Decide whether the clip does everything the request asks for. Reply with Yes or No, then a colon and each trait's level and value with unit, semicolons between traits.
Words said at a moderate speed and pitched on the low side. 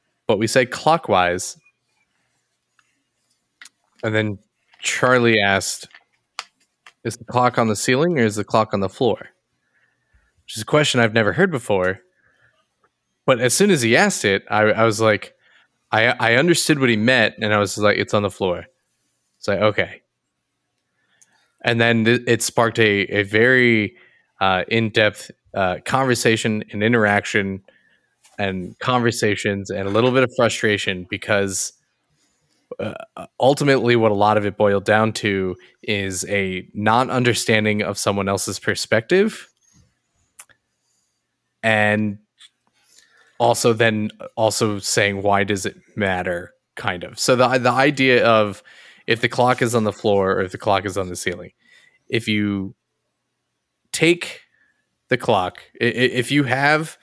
Yes: average, 145 wpm; low, 110 Hz